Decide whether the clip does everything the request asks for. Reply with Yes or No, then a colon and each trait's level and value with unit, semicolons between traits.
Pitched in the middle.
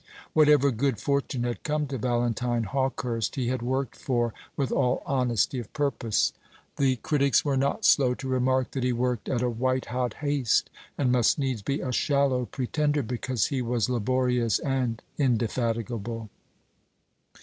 No: low, 125 Hz